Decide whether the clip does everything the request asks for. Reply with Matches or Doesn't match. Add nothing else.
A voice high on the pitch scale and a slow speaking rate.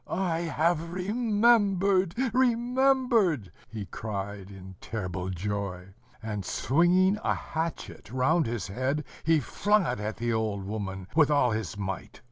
Doesn't match